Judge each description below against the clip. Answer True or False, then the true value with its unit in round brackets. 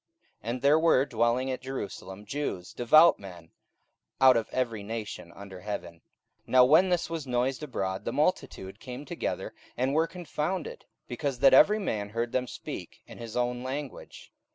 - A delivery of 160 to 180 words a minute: True (170 wpm)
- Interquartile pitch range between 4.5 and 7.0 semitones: True (5.1 semitones)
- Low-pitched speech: True (125 Hz)